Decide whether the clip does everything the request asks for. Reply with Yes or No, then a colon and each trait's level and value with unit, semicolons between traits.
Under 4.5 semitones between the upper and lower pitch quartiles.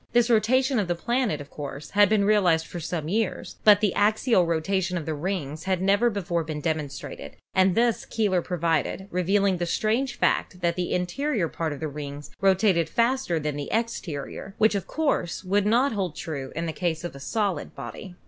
No: average, 4.8 semitones